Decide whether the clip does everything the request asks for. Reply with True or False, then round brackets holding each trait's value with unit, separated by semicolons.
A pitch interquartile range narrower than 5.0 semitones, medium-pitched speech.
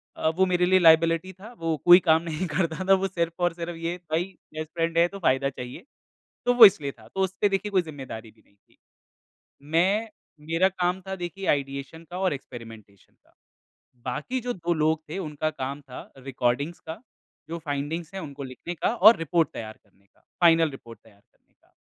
True (4.4 semitones; 165 Hz)